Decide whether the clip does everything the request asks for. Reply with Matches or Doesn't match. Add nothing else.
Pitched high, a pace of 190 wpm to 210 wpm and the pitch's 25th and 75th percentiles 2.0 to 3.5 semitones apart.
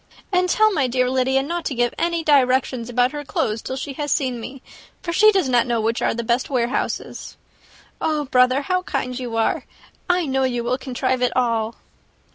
Matches